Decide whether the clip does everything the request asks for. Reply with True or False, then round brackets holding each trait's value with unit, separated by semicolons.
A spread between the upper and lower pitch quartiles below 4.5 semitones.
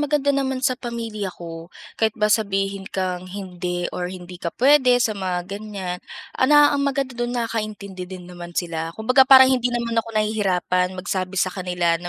False (5.0 semitones)